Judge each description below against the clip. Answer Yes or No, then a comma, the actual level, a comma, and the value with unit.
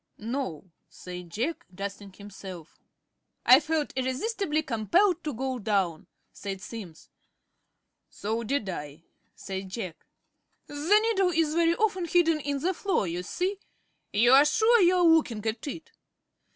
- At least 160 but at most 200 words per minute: No, average, 140 wpm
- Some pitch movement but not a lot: No, wide, 8.9 semitones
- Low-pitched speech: No, very high, 260 Hz